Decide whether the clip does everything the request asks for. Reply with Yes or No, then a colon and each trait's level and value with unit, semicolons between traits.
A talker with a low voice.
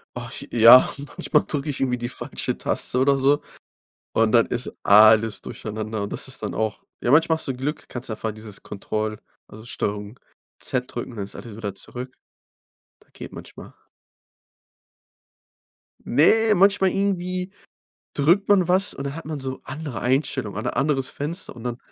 Yes: low, 130 Hz